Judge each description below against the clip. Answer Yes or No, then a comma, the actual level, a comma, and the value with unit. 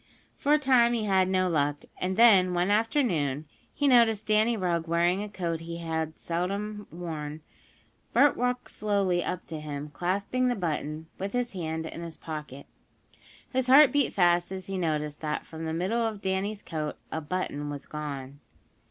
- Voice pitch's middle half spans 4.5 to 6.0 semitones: Yes, average, 5.0 semitones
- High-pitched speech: No, medium, 180 Hz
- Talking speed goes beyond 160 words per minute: Yes, average, 180 wpm